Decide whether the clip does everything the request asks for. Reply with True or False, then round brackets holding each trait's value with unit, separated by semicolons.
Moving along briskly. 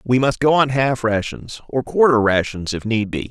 True (220 wpm)